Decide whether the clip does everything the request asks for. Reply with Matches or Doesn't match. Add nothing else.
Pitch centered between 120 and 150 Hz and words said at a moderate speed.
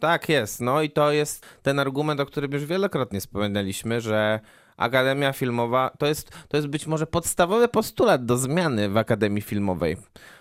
Doesn't match